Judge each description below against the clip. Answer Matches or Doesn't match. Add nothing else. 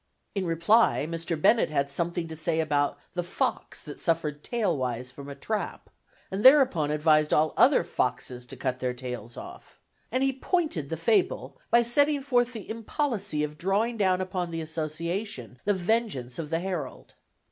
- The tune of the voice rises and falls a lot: Matches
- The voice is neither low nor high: Matches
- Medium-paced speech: Matches